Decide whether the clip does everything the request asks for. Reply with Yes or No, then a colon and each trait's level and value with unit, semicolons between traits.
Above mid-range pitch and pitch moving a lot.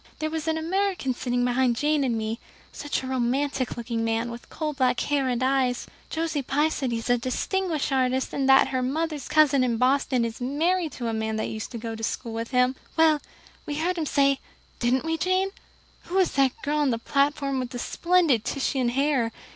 No: very high, 265 Hz; average, 3.7 semitones